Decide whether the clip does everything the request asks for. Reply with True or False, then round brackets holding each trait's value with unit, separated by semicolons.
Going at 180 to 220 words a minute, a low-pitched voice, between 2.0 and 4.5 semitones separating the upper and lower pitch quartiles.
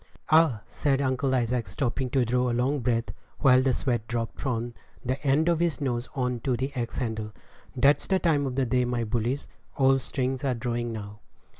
True (190 wpm; 125 Hz; 2.4 semitones)